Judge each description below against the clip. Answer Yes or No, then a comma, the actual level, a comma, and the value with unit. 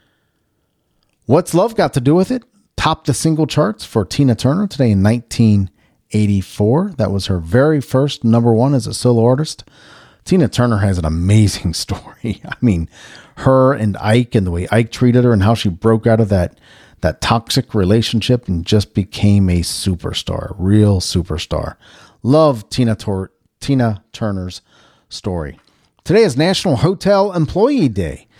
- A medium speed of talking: Yes, average, 155 wpm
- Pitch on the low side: Yes, low, 115 Hz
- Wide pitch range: Yes, wide, 5.9 semitones